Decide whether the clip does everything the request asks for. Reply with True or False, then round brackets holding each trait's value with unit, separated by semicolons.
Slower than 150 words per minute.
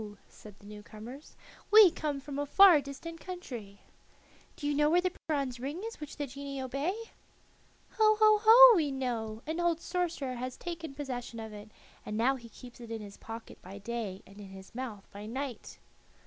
False (190 wpm)